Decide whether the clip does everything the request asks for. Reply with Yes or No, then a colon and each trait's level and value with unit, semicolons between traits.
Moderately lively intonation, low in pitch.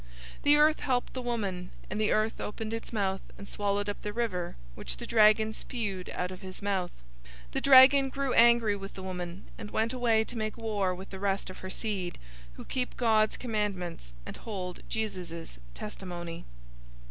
No: average, 3.5 semitones; high, 210 Hz